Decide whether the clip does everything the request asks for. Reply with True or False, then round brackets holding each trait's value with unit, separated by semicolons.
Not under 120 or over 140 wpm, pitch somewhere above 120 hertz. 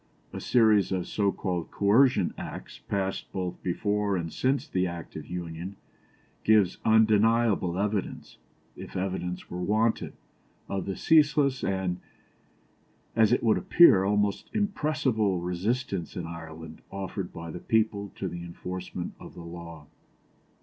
False (135 wpm; 95 Hz)